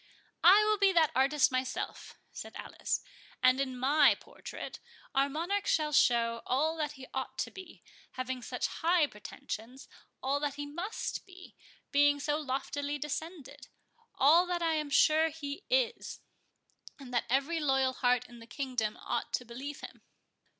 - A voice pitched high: Yes, very high, 285 Hz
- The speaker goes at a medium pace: Yes, average, 150 wpm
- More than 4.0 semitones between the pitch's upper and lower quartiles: No, average, 3.7 semitones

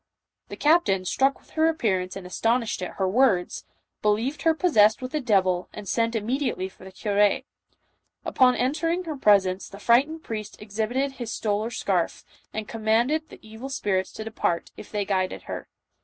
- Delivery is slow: No, average, 180 wpm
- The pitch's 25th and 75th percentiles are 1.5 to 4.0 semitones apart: No, average, 5.1 semitones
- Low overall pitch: No, high, 220 Hz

